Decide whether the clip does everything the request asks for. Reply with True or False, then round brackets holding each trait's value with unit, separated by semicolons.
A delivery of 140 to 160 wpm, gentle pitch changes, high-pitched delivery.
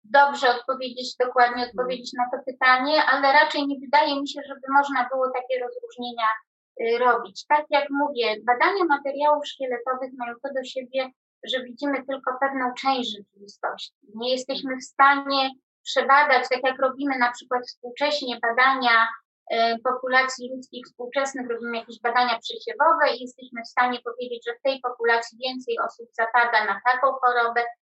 True (150 wpm; 2.1 semitones; 255 Hz)